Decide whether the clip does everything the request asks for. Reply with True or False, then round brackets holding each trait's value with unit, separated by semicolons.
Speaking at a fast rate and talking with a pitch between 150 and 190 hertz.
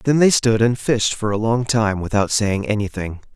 False (215 wpm; 110 Hz)